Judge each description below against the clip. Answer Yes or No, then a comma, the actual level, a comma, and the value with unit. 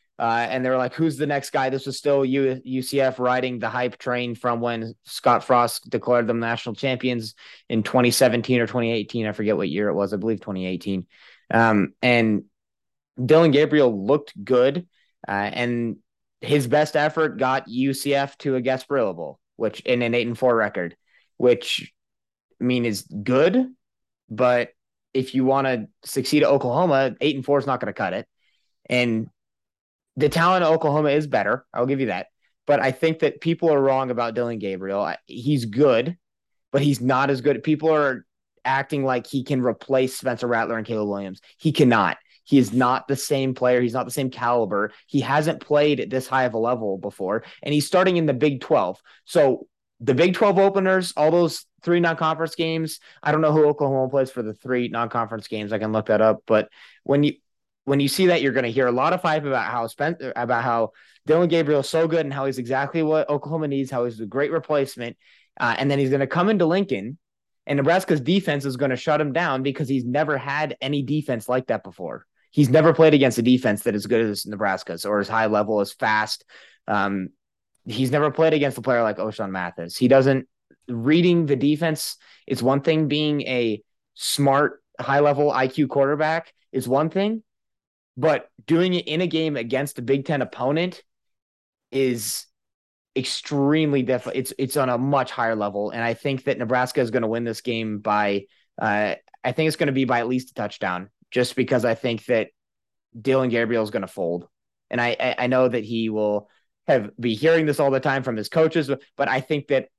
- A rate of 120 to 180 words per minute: No, average, 200 wpm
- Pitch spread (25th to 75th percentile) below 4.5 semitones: Yes, average, 3.9 semitones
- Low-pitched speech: Yes, low, 130 Hz